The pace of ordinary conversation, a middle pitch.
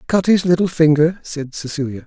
Yes: average, 175 wpm; medium, 160 Hz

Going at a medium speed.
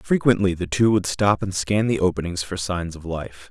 No: fast, 225 wpm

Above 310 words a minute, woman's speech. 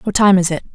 Yes: fast, 325 wpm; female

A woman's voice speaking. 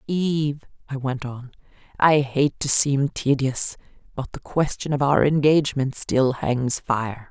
Yes: female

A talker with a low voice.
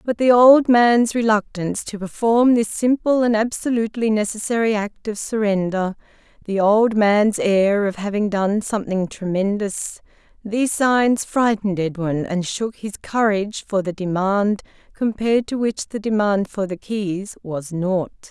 No: high, 210 Hz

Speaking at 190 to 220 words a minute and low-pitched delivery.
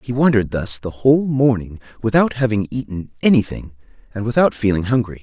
No: average, 160 wpm; low, 115 Hz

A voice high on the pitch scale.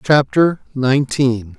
No: low, 135 Hz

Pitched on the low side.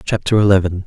Yes: very low, 95 Hz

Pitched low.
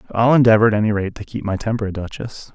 Yes: low, 110 Hz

